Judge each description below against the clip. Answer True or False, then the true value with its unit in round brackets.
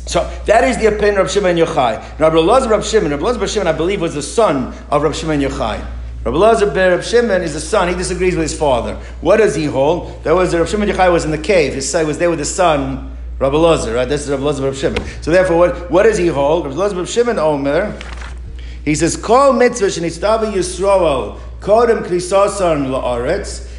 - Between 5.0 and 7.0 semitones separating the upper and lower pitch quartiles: True (5.3 semitones)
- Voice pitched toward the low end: False (170 Hz)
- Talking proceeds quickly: True (210 wpm)